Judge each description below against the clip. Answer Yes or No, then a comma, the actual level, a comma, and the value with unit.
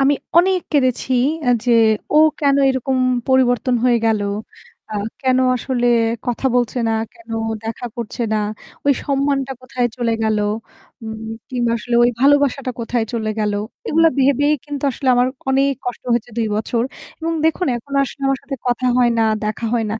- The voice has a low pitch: No, very high, 255 Hz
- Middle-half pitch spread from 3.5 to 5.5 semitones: No, average, 2.8 semitones